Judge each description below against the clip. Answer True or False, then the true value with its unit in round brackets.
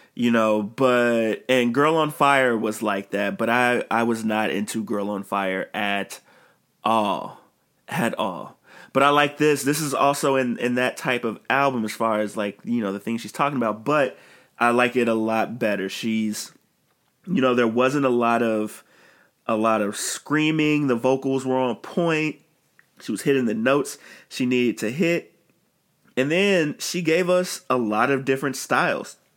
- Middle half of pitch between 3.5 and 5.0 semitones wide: True (4.3 semitones)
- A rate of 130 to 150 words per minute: False (185 wpm)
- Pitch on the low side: True (120 Hz)